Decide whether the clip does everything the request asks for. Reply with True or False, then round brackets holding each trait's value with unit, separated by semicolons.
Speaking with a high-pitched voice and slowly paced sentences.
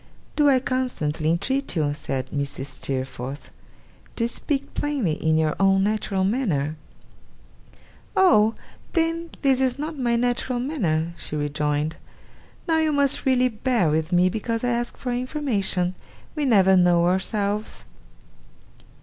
True (210 Hz; 130 wpm)